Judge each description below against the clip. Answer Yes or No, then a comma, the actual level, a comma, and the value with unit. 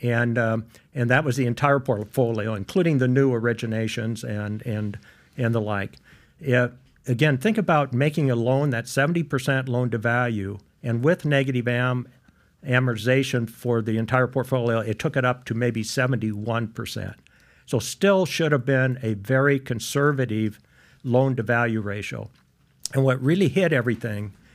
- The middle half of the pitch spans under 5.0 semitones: Yes, average, 2.9 semitones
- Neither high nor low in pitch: No, low, 125 Hz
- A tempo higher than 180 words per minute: No, average, 150 wpm